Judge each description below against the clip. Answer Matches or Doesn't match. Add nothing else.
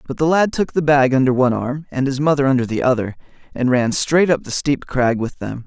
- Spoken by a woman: Doesn't match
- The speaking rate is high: Matches